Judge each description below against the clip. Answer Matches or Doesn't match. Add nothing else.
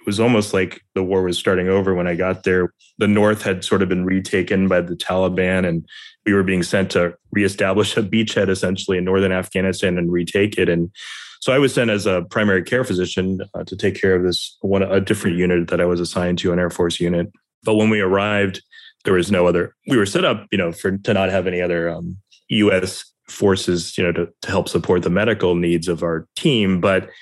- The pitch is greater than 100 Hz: Doesn't match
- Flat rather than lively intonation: Matches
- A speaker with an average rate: Doesn't match